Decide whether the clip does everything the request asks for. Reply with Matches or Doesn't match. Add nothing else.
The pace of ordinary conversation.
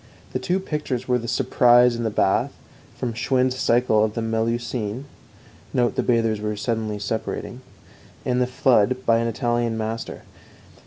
Matches